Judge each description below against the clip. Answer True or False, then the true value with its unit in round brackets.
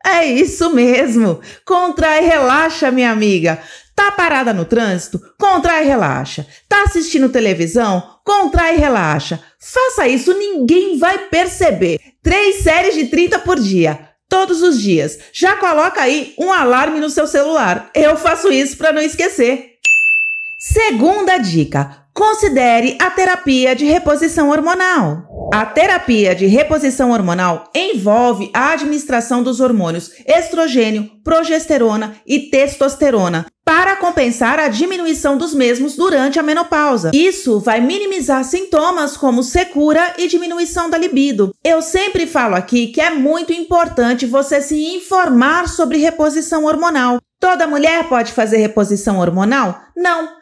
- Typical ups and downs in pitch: False (6.2 semitones)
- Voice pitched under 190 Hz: False (300 Hz)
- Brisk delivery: False (130 wpm)